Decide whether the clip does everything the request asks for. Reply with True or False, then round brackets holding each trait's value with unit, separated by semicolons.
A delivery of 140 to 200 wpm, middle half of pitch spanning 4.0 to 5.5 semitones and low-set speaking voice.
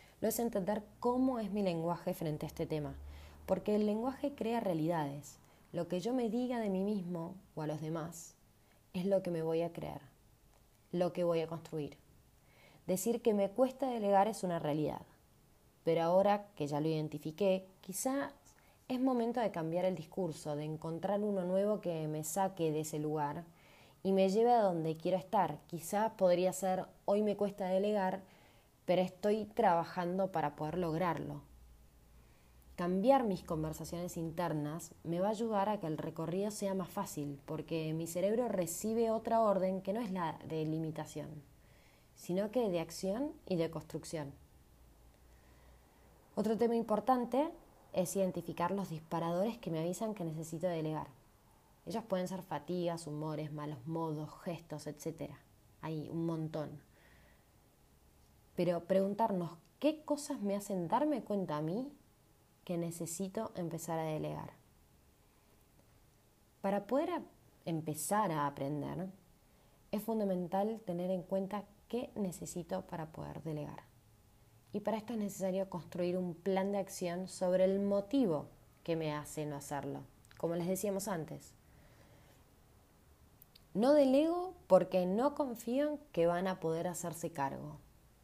False (145 wpm; 4.8 semitones; 175 Hz)